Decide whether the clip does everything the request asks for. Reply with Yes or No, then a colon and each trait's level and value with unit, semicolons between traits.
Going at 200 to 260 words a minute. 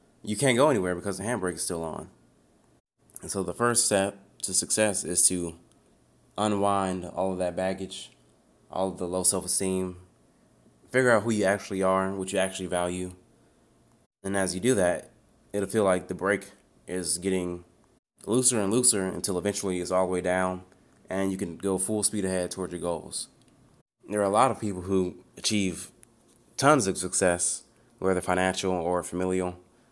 No: average, 175 wpm